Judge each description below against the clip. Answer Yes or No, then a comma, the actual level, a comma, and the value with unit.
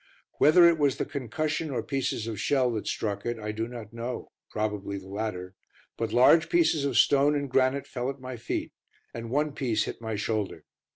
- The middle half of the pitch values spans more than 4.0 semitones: Yes, average, 4.5 semitones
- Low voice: Yes, low, 120 Hz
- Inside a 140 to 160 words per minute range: No, average, 195 wpm